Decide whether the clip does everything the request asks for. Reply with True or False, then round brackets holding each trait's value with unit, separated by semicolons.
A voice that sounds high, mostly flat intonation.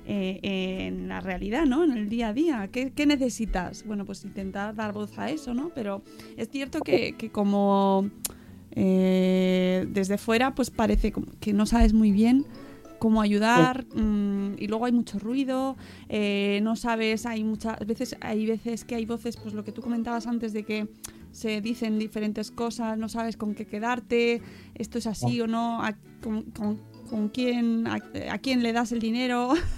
True (220 Hz; 2.3 semitones)